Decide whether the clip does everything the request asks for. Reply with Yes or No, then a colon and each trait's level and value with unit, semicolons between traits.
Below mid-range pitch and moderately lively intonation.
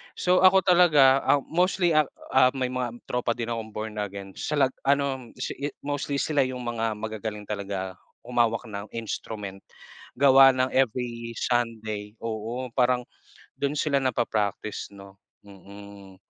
Yes: low, 120 Hz; average, 4.1 semitones